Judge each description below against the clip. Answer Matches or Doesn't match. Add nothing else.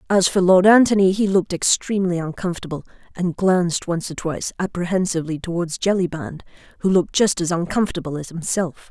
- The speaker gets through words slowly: Doesn't match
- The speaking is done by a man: Doesn't match